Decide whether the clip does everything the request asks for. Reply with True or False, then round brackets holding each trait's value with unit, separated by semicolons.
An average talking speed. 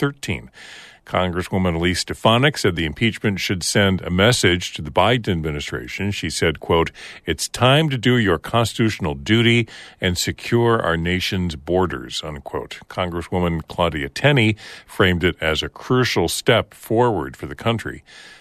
True (145 wpm)